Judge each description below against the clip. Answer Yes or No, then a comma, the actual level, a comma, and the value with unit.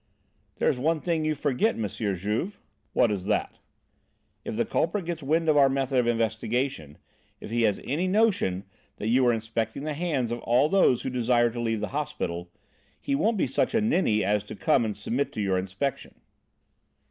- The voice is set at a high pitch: No, low, 125 Hz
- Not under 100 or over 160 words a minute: No, average, 195 wpm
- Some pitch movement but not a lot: No, wide, 5.9 semitones